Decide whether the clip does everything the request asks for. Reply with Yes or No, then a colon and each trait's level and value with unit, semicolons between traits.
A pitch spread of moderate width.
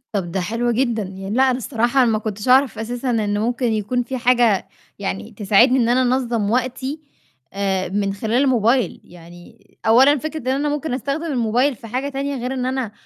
Yes: average, 3.6 semitones